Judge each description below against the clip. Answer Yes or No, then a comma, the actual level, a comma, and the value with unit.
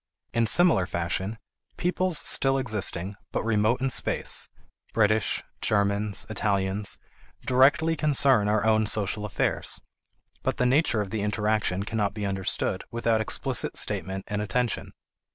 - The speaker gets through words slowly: Yes, slow, 130 wpm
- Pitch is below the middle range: Yes, low, 110 Hz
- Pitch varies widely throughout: No, average, 3.5 semitones